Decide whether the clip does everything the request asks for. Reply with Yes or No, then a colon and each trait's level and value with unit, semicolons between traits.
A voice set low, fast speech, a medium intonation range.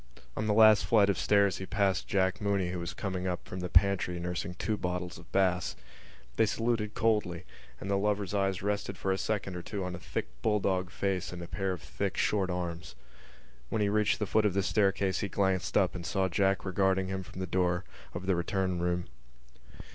No: very low, 95 Hz; fast, 210 wpm; narrow, 2.0 semitones